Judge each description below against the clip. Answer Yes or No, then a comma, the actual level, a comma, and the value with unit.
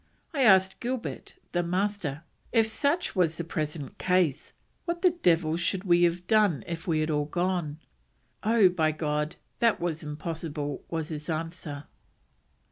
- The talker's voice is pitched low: No, medium, 170 Hz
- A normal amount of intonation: Yes, average, 3.8 semitones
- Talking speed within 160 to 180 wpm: No, average, 150 wpm